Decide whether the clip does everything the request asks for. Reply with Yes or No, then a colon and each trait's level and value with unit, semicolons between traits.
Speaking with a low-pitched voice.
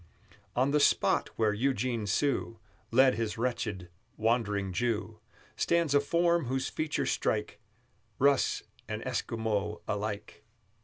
Yes: low, 115 Hz